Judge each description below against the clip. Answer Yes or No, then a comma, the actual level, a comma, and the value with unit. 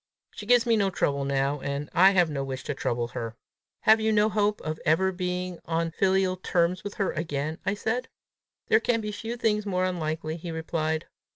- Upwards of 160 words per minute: Yes, average, 200 wpm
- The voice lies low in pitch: No, medium, 180 Hz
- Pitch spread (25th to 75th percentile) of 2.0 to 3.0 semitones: No, average, 4.9 semitones